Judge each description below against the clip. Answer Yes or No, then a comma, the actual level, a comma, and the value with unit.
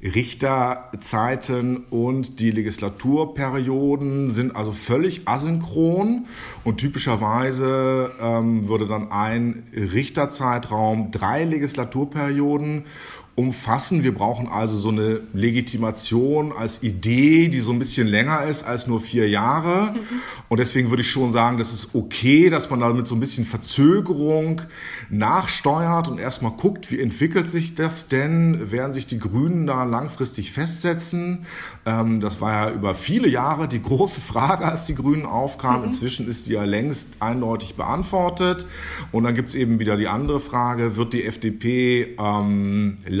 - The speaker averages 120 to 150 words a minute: Yes, average, 145 wpm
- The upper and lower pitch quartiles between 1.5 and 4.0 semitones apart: No, average, 4.5 semitones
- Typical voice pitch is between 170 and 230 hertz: No, low, 125 Hz